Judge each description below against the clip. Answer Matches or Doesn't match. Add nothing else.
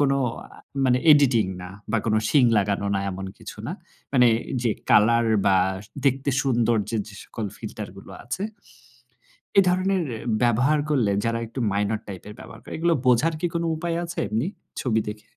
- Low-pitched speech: Matches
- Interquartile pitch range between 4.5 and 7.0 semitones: Matches